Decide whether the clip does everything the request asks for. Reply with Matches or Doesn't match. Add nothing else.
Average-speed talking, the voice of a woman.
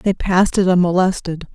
Matches